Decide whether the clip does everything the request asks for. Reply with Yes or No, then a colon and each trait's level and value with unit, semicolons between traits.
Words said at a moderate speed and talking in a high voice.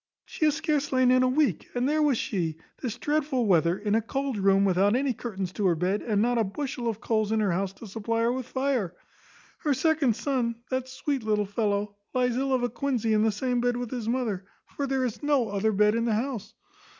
No: fast, 235 wpm; high, 235 Hz